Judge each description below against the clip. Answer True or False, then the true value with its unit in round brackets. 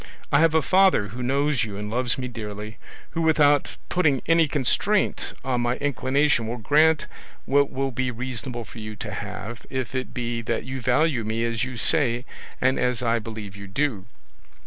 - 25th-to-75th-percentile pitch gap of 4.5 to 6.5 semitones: False (3.9 semitones)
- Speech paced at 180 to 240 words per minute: True (185 wpm)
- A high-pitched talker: False (125 Hz)